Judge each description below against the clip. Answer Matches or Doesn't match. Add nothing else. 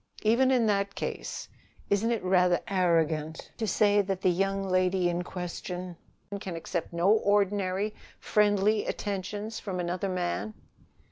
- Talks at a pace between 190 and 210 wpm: Doesn't match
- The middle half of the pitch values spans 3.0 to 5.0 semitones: Doesn't match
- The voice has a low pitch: Doesn't match